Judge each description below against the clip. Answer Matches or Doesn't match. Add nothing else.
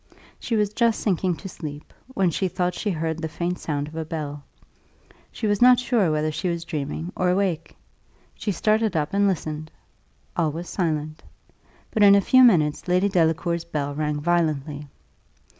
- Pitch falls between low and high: Matches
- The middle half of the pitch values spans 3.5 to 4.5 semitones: Matches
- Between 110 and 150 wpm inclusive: Doesn't match